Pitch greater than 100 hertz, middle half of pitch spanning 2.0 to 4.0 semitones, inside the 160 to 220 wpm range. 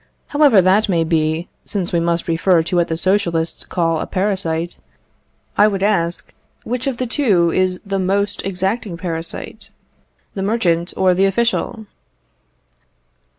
No: medium, 185 Hz; average, 3.3 semitones; average, 145 wpm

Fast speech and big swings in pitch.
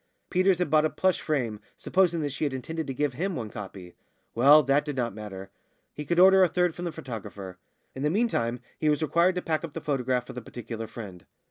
Yes: fast, 230 wpm; wide, 6.3 semitones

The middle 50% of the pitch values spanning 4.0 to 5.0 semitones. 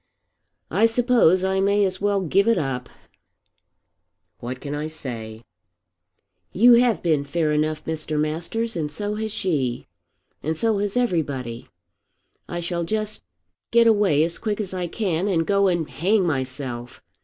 No: wide, 5.5 semitones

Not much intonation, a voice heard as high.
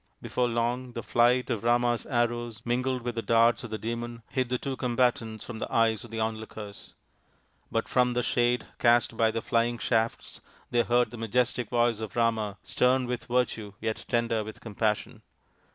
No: narrow, 1.4 semitones; low, 120 Hz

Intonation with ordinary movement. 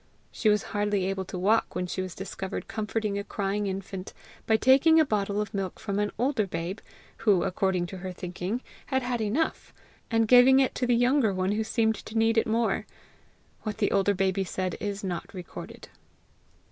Yes: average, 3.0 semitones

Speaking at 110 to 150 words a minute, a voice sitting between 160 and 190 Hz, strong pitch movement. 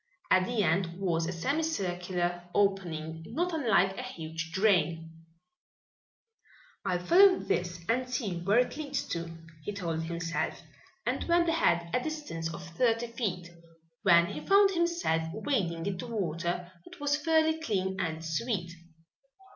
Yes: average, 140 wpm; medium, 185 Hz; wide, 6.9 semitones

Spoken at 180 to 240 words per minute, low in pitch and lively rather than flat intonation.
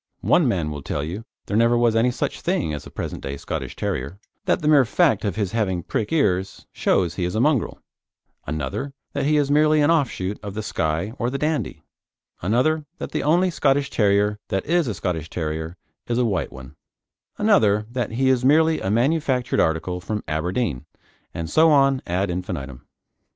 Yes: average, 190 wpm; low, 105 Hz; wide, 7.9 semitones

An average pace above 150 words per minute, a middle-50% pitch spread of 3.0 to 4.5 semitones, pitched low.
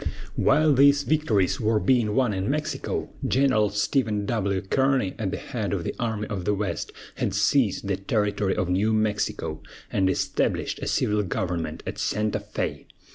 No: average, 165 wpm; average, 4.9 semitones; low, 105 Hz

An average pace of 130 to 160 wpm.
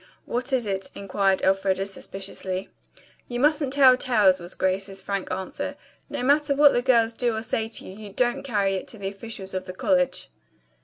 No: average, 185 wpm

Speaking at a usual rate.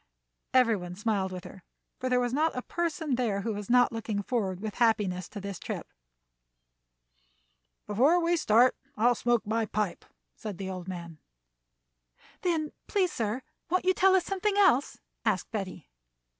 Yes: average, 165 wpm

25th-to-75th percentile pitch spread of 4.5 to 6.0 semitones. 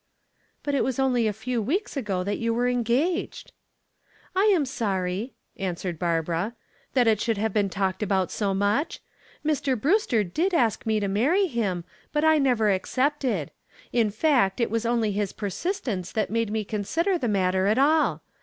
Yes: wide, 5.4 semitones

